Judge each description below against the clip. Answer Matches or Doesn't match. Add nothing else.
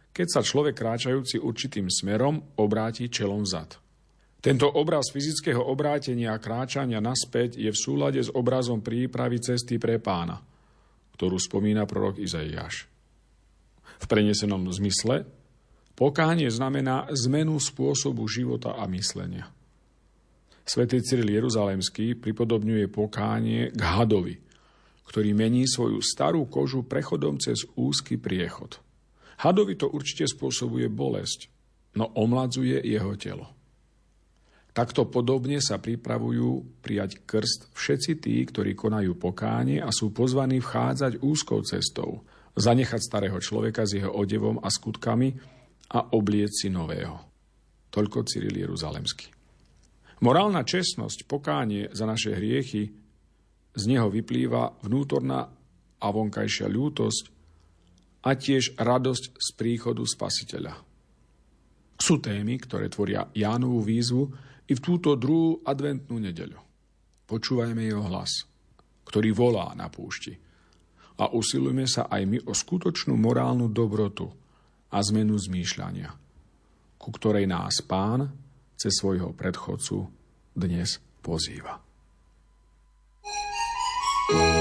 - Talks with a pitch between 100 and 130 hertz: Matches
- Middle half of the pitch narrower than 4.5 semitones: Doesn't match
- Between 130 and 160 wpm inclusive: Doesn't match